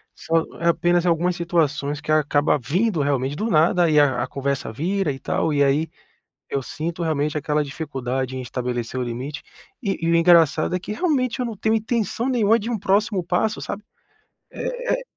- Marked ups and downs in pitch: Yes, wide, 5.8 semitones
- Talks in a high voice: No, medium, 165 Hz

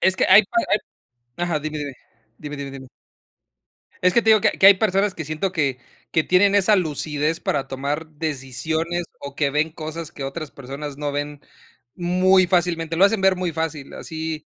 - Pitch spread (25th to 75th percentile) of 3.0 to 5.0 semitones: Yes, average, 3.9 semitones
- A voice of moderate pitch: Yes, medium, 160 Hz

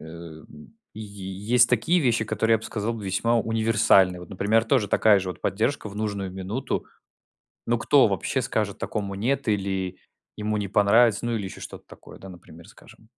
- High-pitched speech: No, low, 105 Hz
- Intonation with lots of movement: No, average, 2.9 semitones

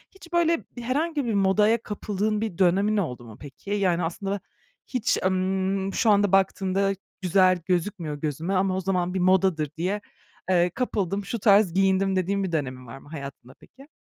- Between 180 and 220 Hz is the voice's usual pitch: Yes, high, 190 Hz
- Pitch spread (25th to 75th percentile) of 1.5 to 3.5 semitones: Yes, average, 2.8 semitones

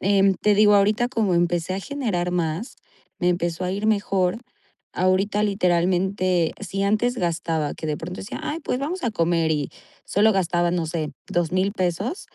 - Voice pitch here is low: No, medium, 185 Hz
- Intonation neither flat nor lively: Yes, average, 3.1 semitones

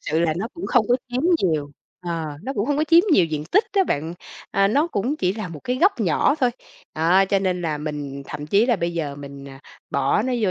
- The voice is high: No, medium, 180 Hz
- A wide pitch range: Yes, wide, 8.2 semitones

